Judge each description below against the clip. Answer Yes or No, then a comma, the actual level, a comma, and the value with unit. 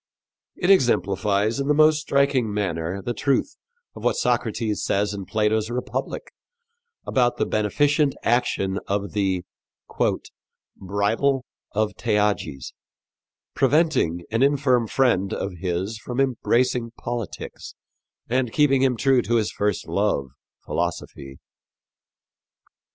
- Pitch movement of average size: Yes, average, 4.9 semitones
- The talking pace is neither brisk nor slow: No, slow, 110 wpm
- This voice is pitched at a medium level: No, low, 115 Hz